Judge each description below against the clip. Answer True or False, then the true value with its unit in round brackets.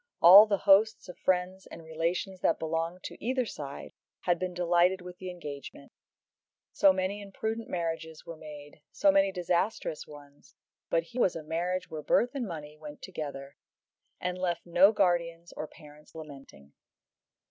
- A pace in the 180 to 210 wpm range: False (160 wpm)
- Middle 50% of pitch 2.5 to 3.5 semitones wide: True (3.2 semitones)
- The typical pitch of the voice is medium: True (175 Hz)